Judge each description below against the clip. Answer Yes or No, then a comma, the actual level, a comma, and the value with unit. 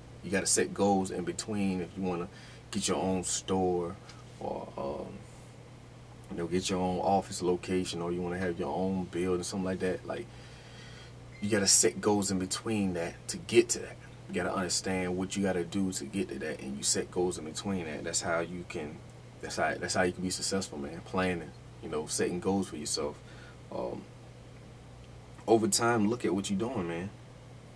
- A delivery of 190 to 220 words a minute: Yes, average, 195 wpm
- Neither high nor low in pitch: No, very low, 95 Hz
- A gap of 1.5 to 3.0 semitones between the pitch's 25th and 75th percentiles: No, average, 3.6 semitones